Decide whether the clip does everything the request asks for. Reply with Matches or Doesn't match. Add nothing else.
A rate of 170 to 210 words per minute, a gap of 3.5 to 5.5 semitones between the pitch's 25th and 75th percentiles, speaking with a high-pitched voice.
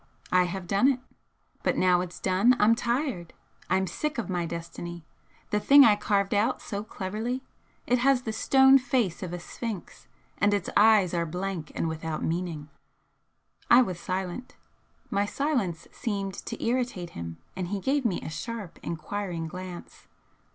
Doesn't match